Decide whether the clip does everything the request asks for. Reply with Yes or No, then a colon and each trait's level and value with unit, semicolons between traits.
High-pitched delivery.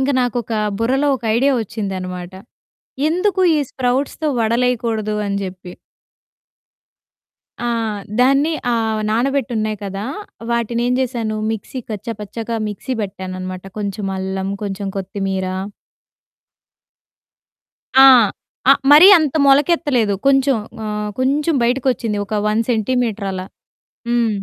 Yes: high, 225 Hz